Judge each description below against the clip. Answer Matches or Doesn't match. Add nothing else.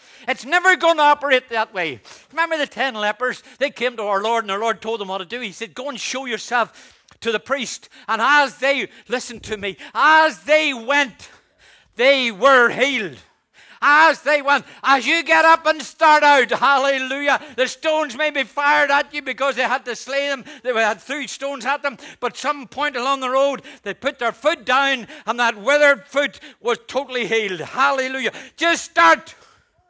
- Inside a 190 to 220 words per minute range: Matches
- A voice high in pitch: Matches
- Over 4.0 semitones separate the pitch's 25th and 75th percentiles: Doesn't match